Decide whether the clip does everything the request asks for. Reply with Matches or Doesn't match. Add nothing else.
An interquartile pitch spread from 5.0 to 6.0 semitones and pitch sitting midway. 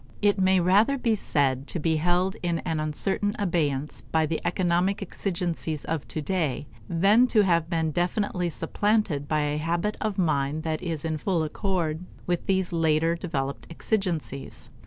Doesn't match